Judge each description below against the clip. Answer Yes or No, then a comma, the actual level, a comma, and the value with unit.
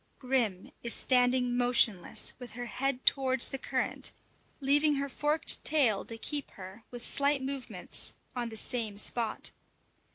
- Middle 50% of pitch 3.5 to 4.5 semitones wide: No, average, 2.8 semitones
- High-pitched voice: Yes, very high, 250 Hz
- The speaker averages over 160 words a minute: No, average, 140 wpm